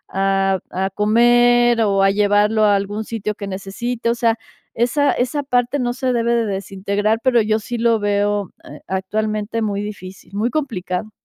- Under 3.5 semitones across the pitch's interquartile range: Yes, average, 3.0 semitones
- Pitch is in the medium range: No, high, 215 Hz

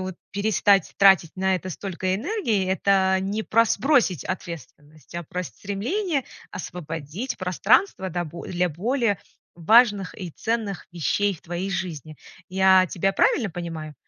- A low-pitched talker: No, high, 190 Hz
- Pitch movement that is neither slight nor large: Yes, average, 3.0 semitones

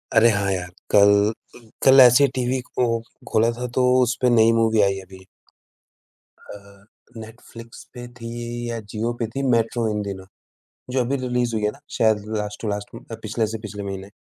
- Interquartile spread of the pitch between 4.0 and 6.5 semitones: No, average, 3.0 semitones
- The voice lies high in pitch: No, low, 115 Hz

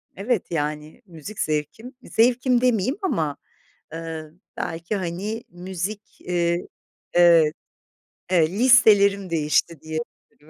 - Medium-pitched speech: Yes, medium, 175 Hz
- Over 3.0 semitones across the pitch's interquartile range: Yes, average, 5.2 semitones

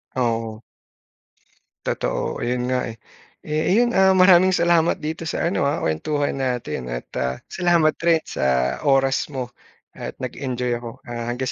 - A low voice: Yes, low, 130 Hz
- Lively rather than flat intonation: Yes, wide, 5.7 semitones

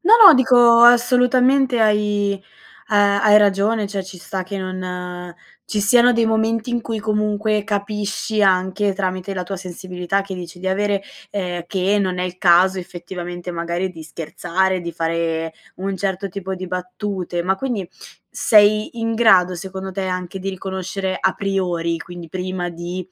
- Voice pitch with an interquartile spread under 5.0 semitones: Yes, average, 2.7 semitones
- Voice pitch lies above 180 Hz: Yes, high, 190 Hz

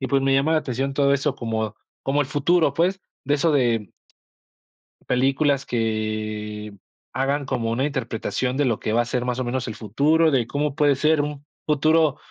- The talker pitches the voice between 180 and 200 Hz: No, low, 135 Hz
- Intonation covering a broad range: No, average, 3.9 semitones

